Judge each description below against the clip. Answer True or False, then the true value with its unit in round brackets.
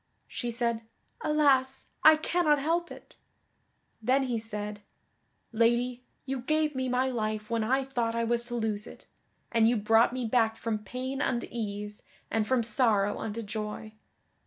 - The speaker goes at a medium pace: True (160 wpm)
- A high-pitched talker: True (235 Hz)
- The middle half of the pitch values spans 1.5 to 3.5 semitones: True (3.0 semitones)